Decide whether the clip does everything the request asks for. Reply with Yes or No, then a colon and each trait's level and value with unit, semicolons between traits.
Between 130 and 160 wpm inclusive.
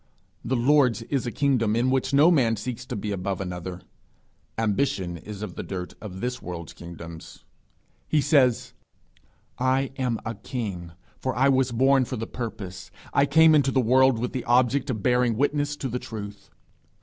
No: average, 175 wpm